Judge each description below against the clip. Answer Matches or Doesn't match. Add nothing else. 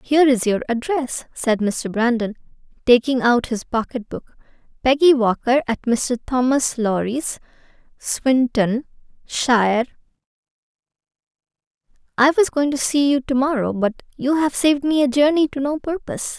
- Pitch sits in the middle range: Doesn't match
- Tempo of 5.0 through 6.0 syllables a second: Doesn't match